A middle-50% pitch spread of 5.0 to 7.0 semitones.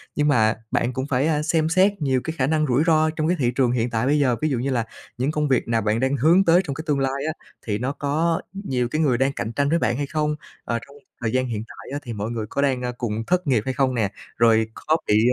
No: average, 4.4 semitones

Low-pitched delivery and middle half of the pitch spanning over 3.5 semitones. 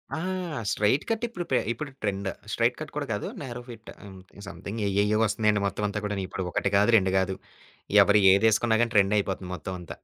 No: low, 105 Hz; average, 3.1 semitones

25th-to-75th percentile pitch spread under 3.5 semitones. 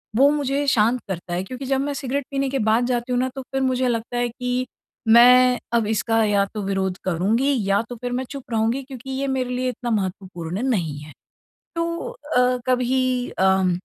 No: average, 3.8 semitones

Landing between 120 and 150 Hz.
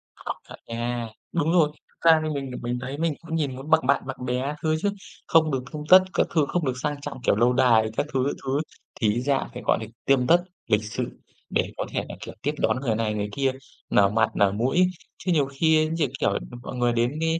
Yes: low, 135 Hz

